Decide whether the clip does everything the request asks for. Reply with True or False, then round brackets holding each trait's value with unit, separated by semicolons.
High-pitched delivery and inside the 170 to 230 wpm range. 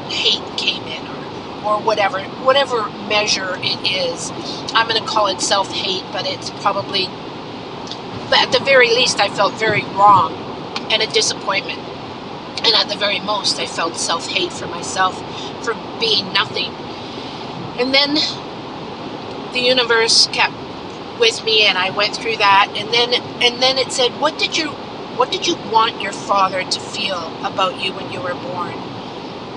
False (240 Hz; 160 wpm)